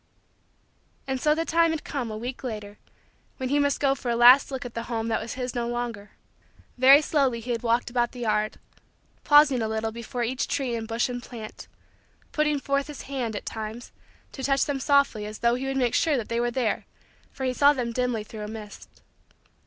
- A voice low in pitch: No, high, 245 Hz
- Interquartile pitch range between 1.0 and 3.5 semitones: Yes, average, 3.1 semitones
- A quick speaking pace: Yes, fast, 215 wpm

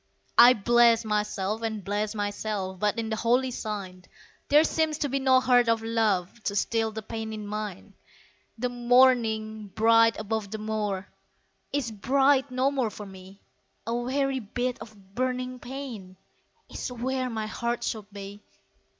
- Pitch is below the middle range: No, high, 225 Hz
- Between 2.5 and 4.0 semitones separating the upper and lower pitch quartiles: Yes, average, 3.1 semitones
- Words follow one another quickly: No, average, 155 wpm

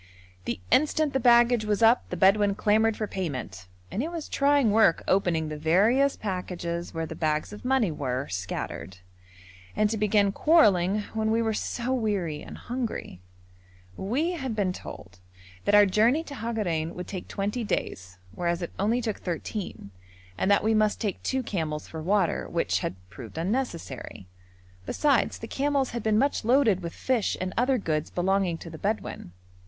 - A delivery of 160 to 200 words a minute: Yes, average, 170 wpm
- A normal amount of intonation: No, wide, 5.7 semitones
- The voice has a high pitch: Yes, high, 205 Hz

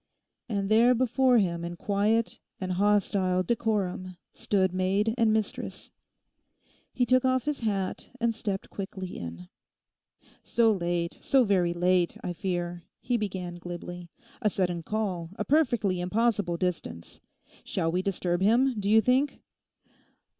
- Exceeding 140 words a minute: No, slow, 135 wpm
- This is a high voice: Yes, high, 195 Hz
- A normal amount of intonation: Yes, average, 4.1 semitones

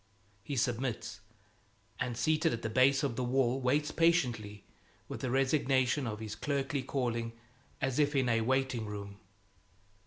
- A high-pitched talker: No, low, 130 Hz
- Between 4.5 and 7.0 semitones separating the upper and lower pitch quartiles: No, average, 3.0 semitones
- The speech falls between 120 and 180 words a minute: Yes, average, 150 wpm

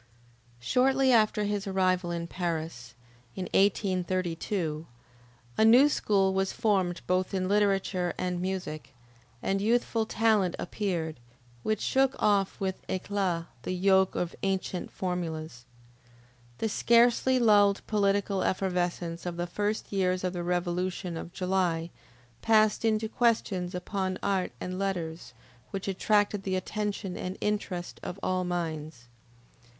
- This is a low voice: No, high, 190 Hz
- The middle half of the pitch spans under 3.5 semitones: Yes, narrow, 2.6 semitones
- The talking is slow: Yes, slow, 125 wpm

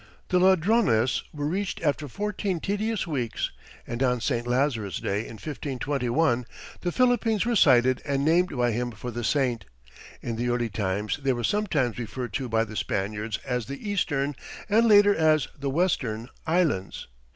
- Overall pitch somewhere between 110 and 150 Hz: Yes, low, 135 Hz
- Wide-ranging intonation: Yes, wide, 7.1 semitones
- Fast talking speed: No, average, 165 wpm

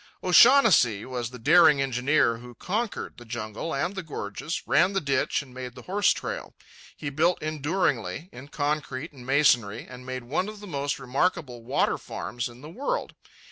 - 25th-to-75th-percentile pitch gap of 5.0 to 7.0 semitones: Yes, wide, 5.5 semitones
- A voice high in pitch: No, medium, 140 Hz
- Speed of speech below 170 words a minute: No, average, 175 wpm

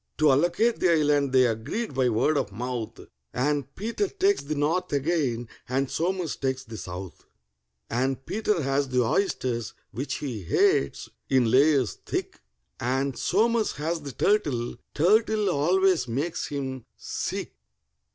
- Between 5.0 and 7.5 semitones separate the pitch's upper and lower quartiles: Yes, wide, 5.6 semitones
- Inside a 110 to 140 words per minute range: Yes, slow, 135 wpm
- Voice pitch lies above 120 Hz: Yes, medium, 140 Hz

